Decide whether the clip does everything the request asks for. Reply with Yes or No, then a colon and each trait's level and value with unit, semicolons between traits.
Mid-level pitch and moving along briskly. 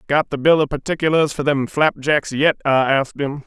Yes: medium, 145 Hz; fast, 210 wpm